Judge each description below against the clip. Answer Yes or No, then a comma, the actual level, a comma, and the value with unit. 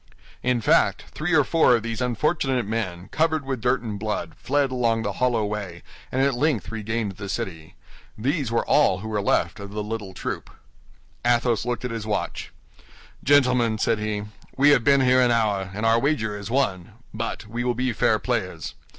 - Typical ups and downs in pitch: Yes, average, 3.4 semitones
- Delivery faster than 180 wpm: Yes, average, 190 wpm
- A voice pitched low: Yes, low, 115 Hz